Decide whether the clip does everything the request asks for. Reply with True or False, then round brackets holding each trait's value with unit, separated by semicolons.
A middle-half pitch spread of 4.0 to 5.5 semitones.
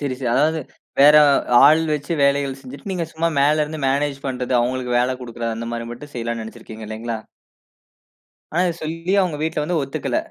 True (4.4 semitones)